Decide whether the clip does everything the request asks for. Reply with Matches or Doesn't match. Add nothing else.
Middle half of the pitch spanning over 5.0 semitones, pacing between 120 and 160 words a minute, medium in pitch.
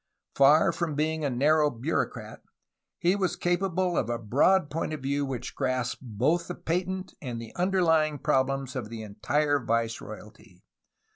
Matches